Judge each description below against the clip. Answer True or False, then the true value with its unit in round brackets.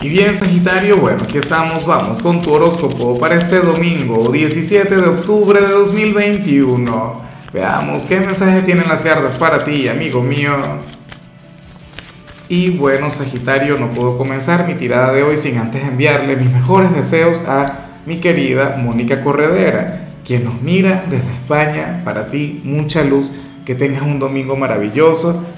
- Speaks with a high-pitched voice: False (150 Hz)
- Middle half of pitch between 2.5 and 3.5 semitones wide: False (4.2 semitones)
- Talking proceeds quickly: False (150 wpm)